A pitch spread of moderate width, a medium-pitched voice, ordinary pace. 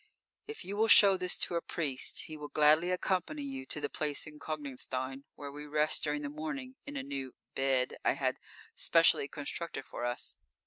Yes: average, 4.5 semitones; medium, 150 Hz; average, 195 wpm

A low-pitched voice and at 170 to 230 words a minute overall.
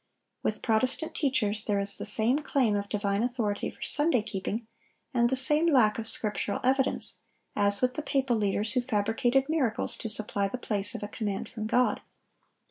No: high, 225 Hz; average, 180 wpm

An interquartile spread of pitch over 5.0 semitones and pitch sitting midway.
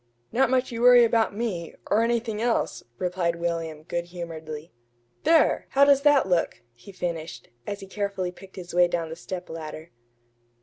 Yes: wide, 5.4 semitones; medium, 180 Hz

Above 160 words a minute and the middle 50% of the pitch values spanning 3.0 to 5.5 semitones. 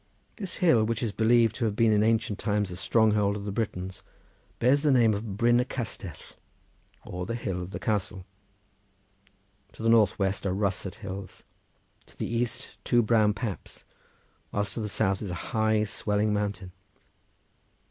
No: average, 170 wpm; narrow, 2.6 semitones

